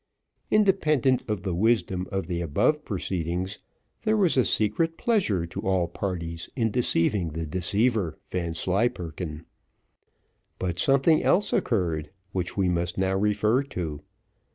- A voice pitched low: Yes, very low, 95 Hz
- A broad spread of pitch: Yes, wide, 6.1 semitones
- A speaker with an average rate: No, slow, 130 wpm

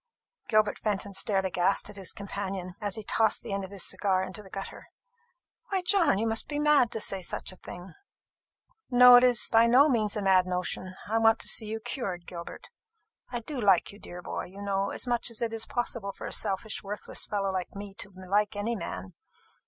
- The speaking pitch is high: Yes, high, 205 Hz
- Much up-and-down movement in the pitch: No, average, 2.9 semitones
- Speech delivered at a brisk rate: Yes, fast, 215 wpm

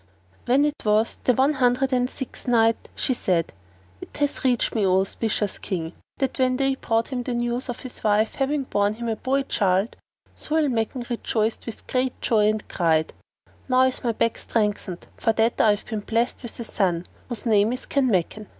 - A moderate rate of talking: Yes, average, 195 wpm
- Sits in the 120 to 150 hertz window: No, high, 230 Hz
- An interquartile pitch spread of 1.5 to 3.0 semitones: No, average, 3.4 semitones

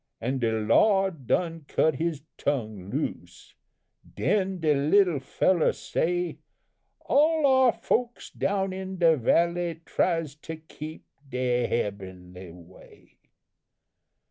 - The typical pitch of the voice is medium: Yes, medium, 160 Hz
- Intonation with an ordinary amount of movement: No, wide, 7.5 semitones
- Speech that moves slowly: Yes, slow, 110 wpm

